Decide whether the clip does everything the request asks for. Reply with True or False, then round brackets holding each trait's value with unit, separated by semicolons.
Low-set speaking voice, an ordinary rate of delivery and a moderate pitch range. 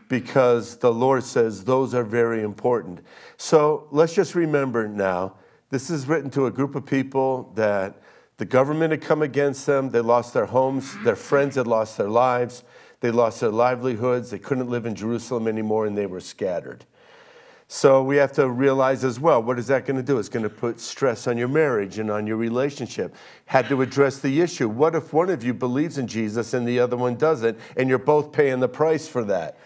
False (130 Hz; 210 wpm; 3.2 semitones)